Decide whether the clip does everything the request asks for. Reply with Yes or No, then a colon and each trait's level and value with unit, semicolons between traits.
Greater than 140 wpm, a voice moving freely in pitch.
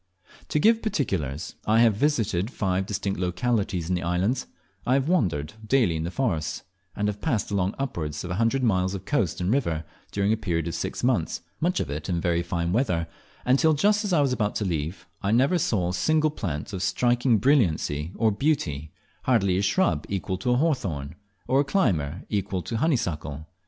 Yes: average, 200 wpm; wide, 7.0 semitones